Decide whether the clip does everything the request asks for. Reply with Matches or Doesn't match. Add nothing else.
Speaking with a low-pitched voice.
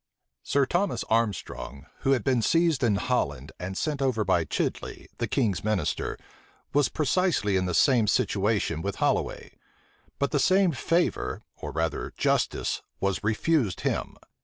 Matches